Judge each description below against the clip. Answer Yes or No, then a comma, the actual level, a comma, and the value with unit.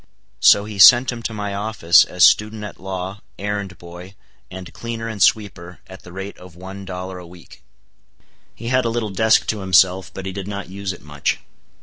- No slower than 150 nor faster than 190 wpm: No, average, 200 wpm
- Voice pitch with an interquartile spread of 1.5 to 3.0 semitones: Yes, narrow, 2.6 semitones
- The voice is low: Yes, very low, 95 Hz